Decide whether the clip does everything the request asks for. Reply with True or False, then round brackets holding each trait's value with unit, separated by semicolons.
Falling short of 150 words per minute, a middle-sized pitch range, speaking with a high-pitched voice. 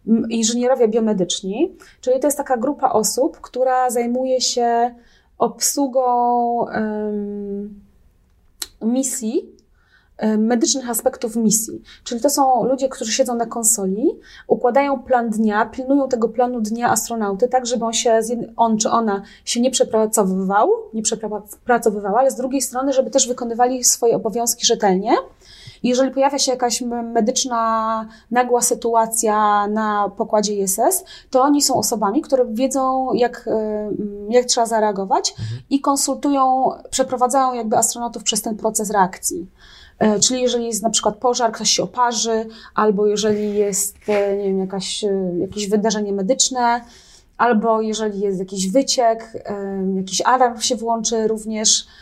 True (130 wpm; 3.0 semitones; 235 Hz)